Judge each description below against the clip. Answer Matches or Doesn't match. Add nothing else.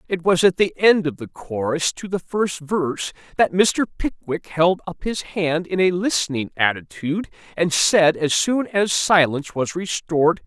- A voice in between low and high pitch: Matches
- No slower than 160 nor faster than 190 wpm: Matches